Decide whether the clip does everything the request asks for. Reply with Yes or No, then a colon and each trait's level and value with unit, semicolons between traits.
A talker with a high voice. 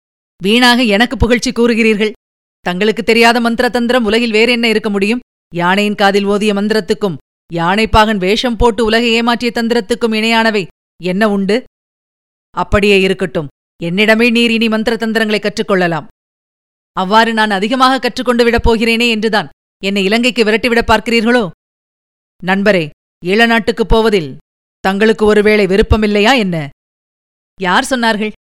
Yes: high, 220 Hz